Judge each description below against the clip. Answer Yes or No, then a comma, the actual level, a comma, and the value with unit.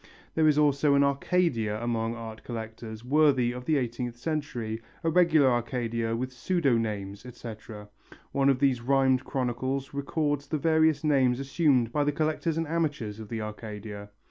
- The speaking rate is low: No, average, 160 wpm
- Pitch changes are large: No, average, 4.3 semitones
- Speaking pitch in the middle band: No, low, 130 Hz